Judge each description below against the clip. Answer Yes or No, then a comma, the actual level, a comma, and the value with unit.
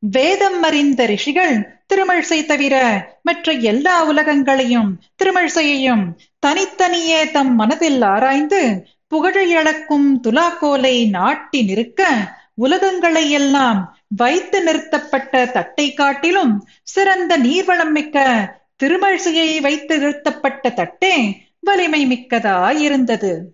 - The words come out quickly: No, average, 80 wpm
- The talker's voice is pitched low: No, very high, 290 Hz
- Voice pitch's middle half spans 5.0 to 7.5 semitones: Yes, average, 5.3 semitones